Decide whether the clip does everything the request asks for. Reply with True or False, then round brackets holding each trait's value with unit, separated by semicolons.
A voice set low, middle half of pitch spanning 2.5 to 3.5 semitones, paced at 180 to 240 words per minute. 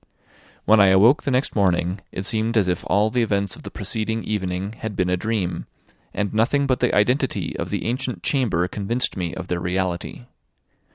False (105 Hz; 3.9 semitones; 190 wpm)